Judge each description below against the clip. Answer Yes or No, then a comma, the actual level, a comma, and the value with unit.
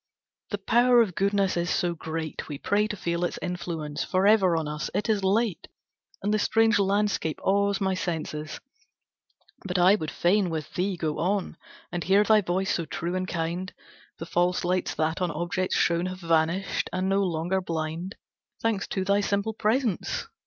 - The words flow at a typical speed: Yes, average, 180 wpm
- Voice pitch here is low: No, medium, 185 Hz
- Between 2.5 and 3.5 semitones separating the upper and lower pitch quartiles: Yes, average, 3.0 semitones